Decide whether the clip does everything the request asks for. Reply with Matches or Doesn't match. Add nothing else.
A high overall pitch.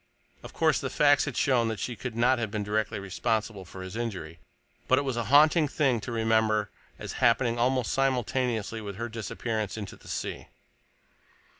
Doesn't match